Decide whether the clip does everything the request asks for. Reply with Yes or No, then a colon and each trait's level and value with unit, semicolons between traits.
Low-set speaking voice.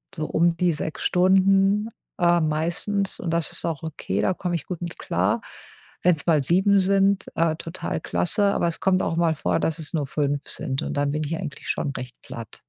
No: medium, 170 Hz